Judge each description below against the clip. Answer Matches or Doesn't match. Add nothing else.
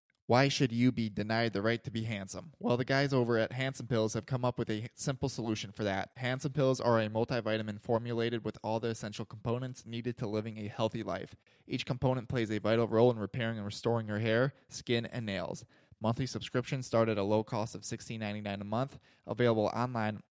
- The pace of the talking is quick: Matches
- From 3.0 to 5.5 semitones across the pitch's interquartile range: Doesn't match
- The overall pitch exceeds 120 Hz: Doesn't match